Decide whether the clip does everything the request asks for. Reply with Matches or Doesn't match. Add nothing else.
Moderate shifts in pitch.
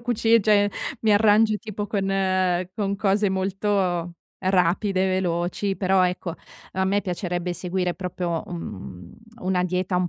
Doesn't match